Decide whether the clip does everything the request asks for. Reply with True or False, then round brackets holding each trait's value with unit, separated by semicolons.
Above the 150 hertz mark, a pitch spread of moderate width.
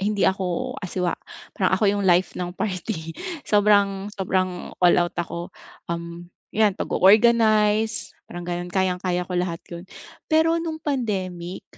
True (190 Hz; 3.1 semitones)